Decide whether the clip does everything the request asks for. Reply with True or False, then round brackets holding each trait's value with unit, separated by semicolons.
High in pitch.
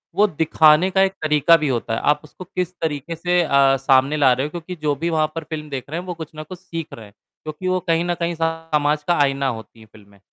False (155 Hz)